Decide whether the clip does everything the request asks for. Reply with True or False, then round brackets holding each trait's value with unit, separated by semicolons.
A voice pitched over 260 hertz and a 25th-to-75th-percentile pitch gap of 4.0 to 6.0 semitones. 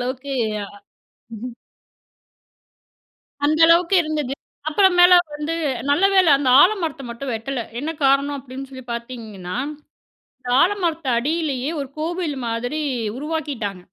True (280 Hz; 4.5 semitones)